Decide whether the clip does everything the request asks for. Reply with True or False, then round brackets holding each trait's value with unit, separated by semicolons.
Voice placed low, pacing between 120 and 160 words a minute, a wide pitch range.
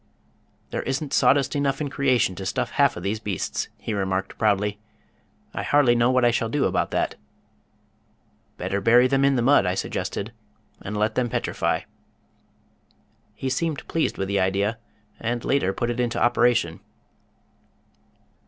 False (120 Hz; 155 wpm; 4.9 semitones)